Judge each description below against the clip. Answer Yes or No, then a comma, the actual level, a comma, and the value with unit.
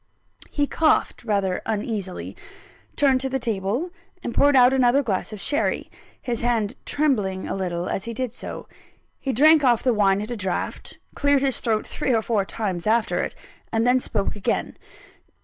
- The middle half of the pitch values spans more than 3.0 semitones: Yes, average, 4.5 semitones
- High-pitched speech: Yes, high, 230 Hz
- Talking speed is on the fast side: No, average, 175 wpm